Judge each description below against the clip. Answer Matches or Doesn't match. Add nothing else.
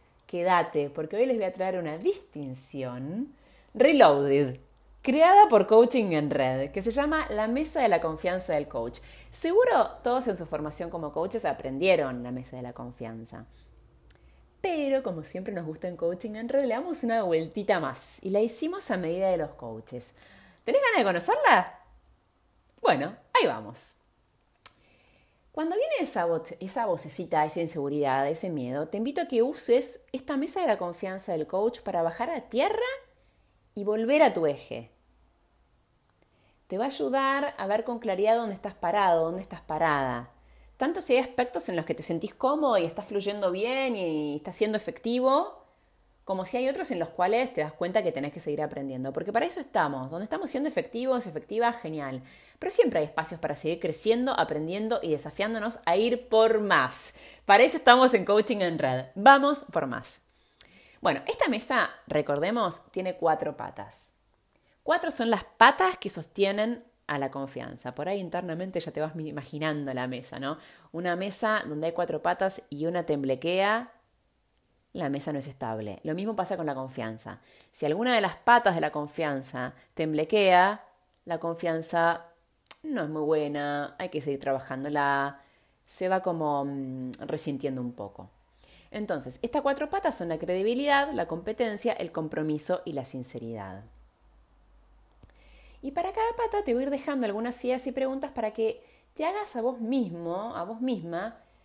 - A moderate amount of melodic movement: Doesn't match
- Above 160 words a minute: Matches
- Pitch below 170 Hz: Doesn't match